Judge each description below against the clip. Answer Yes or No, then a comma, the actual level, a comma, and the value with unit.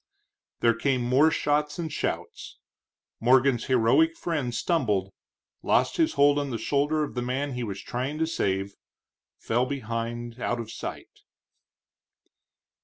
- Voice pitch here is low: Yes, low, 130 Hz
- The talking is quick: No, slow, 135 wpm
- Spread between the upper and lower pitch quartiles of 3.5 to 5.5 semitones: Yes, average, 3.8 semitones